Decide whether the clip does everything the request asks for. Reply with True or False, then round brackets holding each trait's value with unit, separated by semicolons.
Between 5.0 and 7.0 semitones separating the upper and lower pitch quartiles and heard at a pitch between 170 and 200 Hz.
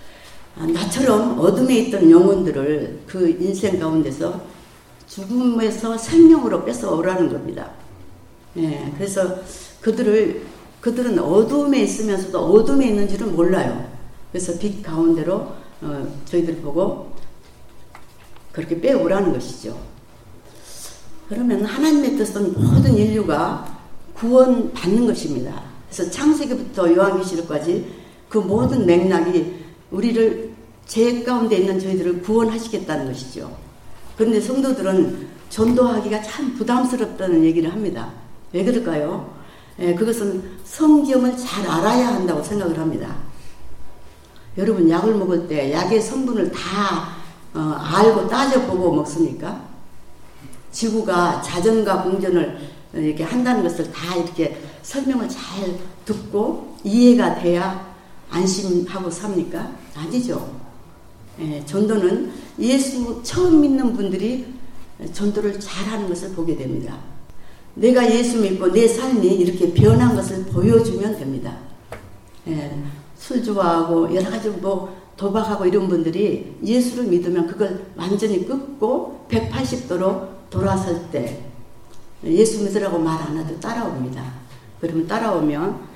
True (5.3 semitones; 190 Hz)